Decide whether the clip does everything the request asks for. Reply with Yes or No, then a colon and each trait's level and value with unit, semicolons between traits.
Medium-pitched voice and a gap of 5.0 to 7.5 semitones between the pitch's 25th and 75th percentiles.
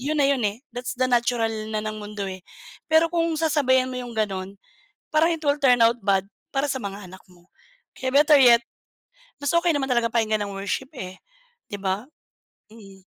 No: high, 240 Hz; average, 5.3 semitones